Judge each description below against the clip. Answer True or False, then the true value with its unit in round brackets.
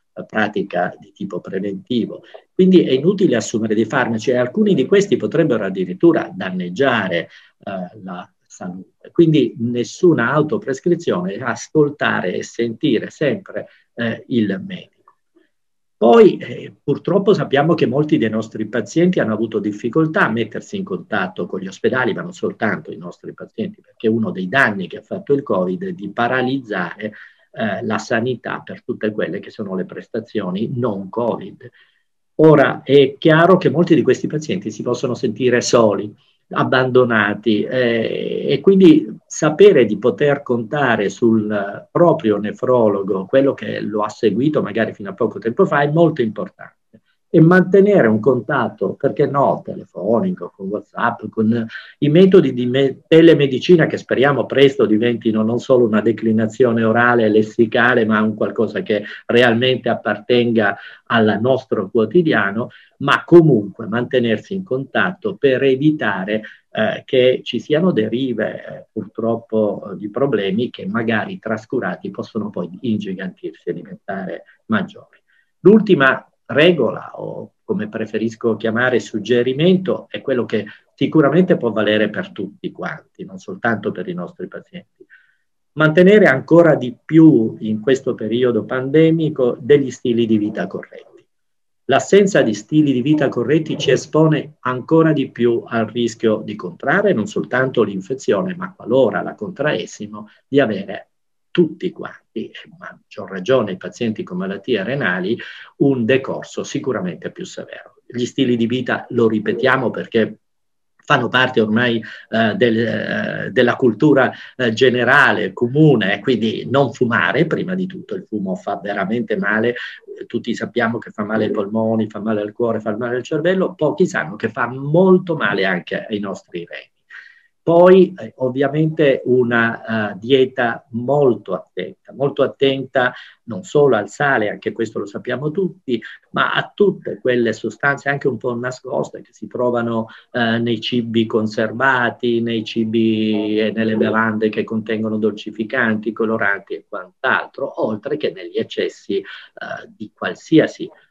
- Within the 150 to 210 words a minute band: False (140 wpm)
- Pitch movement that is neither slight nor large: False (6.0 semitones)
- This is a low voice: True (125 Hz)